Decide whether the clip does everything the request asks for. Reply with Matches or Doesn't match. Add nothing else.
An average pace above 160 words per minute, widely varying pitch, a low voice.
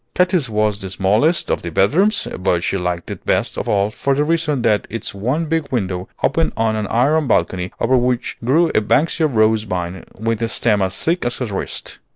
Matches